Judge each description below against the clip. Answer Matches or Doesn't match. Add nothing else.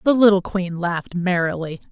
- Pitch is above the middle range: Doesn't match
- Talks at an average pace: Matches